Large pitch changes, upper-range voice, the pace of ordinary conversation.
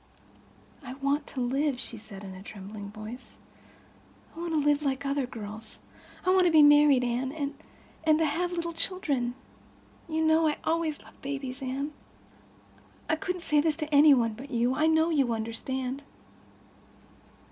No: average, 4.3 semitones; very high, 280 Hz; average, 155 wpm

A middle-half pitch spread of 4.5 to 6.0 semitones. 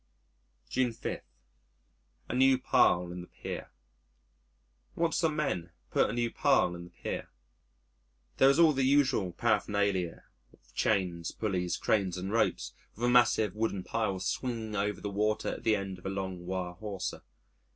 Yes: average, 4.8 semitones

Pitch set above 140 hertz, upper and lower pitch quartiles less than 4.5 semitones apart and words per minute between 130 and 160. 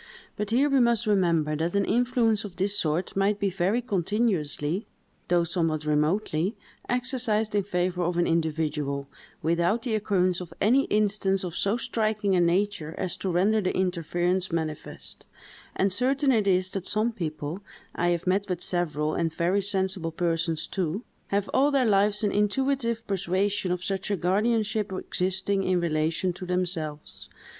Yes: high, 190 Hz; average, 3.6 semitones; average, 155 wpm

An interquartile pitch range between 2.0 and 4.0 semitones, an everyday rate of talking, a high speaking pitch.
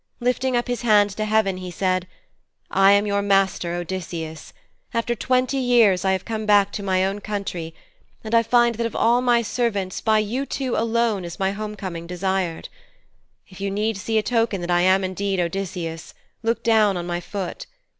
Yes: average, 3.6 semitones; average, 185 wpm; high, 200 Hz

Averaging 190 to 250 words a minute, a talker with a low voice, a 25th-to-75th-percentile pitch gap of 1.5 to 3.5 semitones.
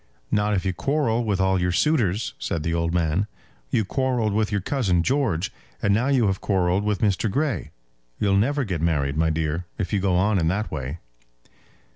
No: average, 195 wpm; low, 100 Hz; average, 4.0 semitones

